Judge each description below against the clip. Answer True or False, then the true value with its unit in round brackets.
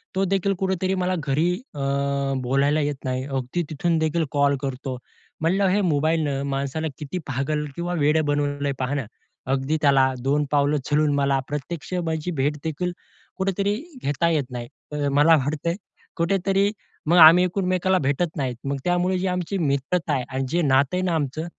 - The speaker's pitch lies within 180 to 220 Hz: False (150 Hz)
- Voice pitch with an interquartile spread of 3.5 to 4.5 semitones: True (4.0 semitones)